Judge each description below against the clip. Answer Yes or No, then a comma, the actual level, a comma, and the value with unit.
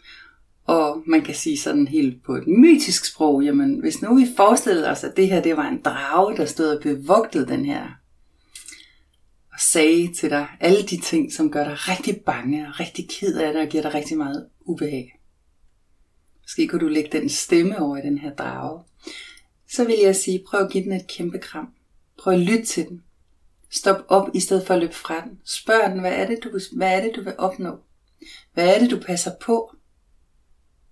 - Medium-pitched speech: Yes, medium, 180 Hz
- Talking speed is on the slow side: No, average, 210 wpm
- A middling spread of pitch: No, wide, 6.8 semitones